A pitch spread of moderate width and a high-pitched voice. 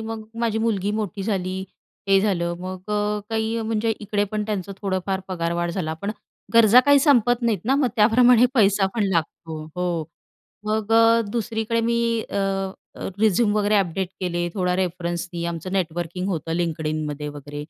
Yes: average, 4.2 semitones; high, 200 Hz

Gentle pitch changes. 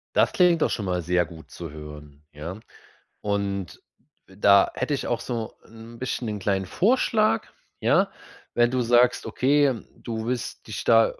No: wide, 5.8 semitones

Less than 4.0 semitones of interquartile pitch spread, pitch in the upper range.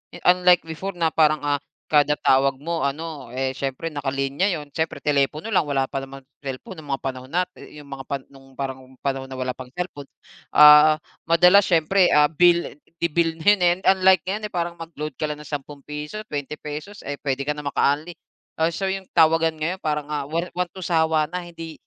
No: average, 3.5 semitones; medium, 155 Hz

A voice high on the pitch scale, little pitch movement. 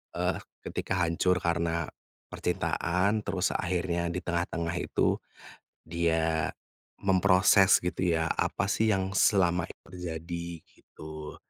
No: very low, 85 Hz; narrow, 1.9 semitones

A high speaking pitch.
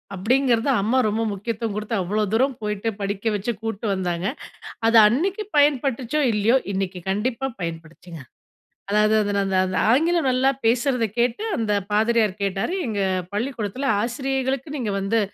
Yes: high, 225 Hz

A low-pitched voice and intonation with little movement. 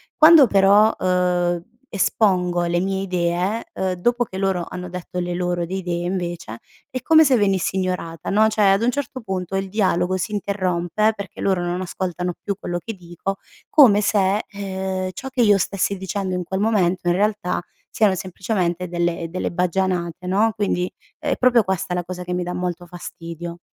No: medium, 185 Hz; narrow, 2.3 semitones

